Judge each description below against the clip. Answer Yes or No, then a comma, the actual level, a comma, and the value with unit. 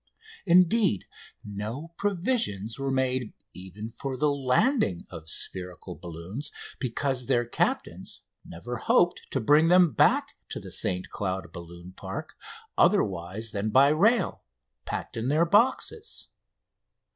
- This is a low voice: Yes, low, 125 Hz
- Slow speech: Yes, slow, 120 wpm